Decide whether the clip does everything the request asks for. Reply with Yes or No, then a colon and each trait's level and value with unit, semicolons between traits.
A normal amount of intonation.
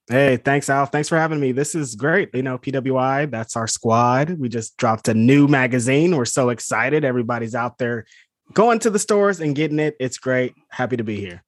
Yes: average, 3.3 semitones